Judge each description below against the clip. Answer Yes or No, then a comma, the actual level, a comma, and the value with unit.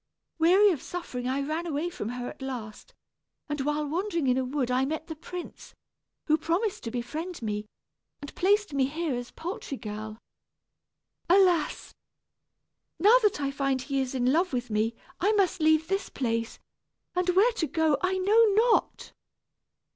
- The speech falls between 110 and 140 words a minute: No, average, 165 wpm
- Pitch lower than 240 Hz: No, very high, 310 Hz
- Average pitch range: No, wide, 5.9 semitones